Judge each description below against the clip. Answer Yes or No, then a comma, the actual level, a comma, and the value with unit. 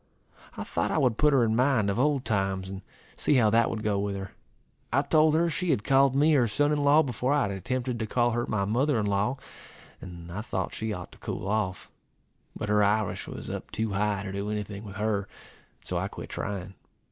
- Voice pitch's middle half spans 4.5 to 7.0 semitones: Yes, average, 4.9 semitones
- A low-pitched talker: Yes, low, 110 Hz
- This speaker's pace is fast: Yes, fast, 235 wpm